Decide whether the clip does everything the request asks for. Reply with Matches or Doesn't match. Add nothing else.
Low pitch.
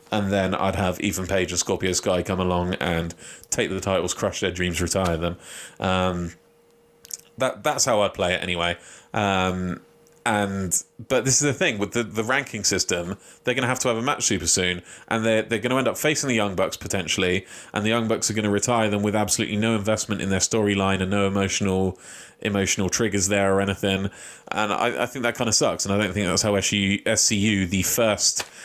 Matches